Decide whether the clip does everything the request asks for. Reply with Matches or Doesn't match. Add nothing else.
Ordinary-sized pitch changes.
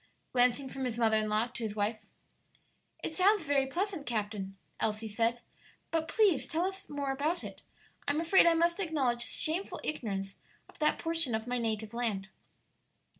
Doesn't match